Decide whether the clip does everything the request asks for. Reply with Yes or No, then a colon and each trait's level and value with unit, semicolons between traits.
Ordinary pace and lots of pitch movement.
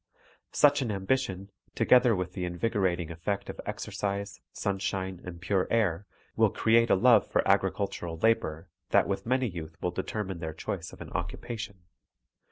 No: average, 160 wpm; average, 4.0 semitones